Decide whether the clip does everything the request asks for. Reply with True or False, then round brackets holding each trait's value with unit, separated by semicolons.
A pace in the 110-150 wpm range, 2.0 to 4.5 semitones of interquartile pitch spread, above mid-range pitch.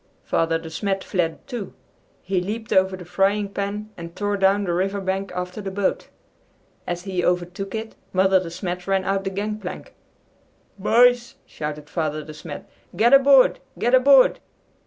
False (165 wpm; 2.7 semitones; 195 Hz)